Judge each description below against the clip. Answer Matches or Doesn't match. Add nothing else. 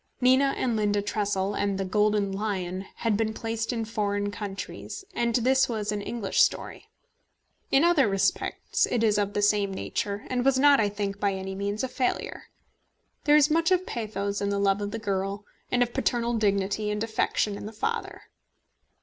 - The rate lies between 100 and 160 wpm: Doesn't match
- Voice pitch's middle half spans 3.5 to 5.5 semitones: Doesn't match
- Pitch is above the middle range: Matches